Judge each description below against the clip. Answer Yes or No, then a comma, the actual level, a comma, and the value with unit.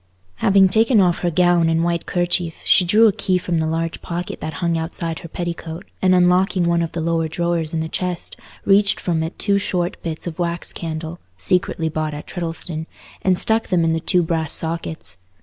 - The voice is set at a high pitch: No, medium, 170 Hz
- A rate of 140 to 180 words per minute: No, average, 195 wpm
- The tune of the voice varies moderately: No, narrow, 1.9 semitones